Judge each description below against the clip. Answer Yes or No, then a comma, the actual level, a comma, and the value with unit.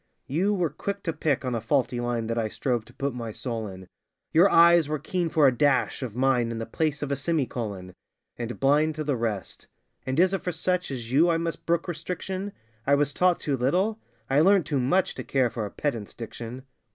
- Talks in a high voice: No, medium, 140 Hz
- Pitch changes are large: Yes, wide, 5.8 semitones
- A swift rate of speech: Yes, fast, 225 wpm